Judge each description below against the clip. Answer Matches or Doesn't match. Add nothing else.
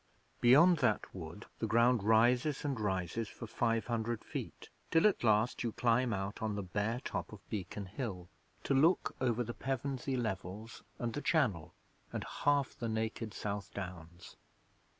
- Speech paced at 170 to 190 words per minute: Doesn't match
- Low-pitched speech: Matches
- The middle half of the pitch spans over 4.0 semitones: Doesn't match